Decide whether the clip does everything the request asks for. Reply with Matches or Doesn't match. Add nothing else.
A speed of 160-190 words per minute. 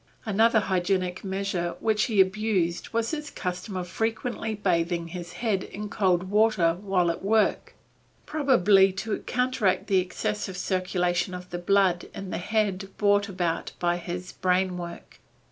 Doesn't match